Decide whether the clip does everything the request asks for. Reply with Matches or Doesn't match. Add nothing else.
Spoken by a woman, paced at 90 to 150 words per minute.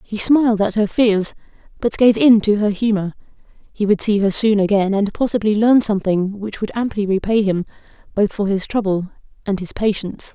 Doesn't match